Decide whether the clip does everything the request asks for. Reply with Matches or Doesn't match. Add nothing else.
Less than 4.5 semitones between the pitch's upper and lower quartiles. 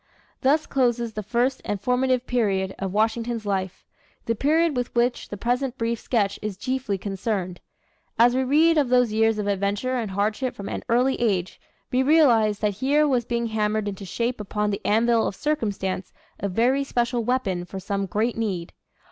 Matches